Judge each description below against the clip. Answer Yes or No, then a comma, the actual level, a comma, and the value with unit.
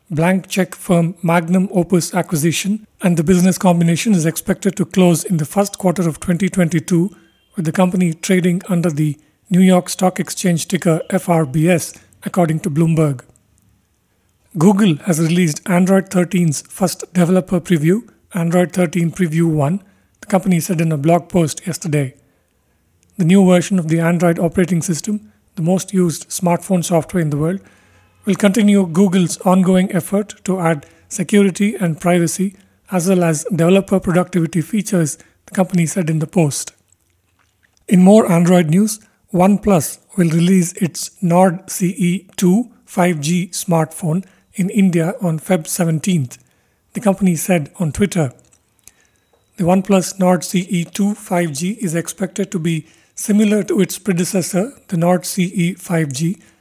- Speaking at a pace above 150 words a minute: No, average, 140 wpm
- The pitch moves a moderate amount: No, narrow, 2.3 semitones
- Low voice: No, medium, 180 Hz